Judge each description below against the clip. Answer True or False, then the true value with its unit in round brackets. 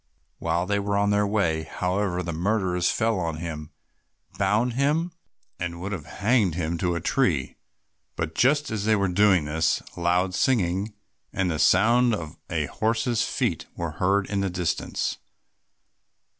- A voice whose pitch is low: True (95 Hz)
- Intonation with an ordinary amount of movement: True (4.0 semitones)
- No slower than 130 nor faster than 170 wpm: True (155 wpm)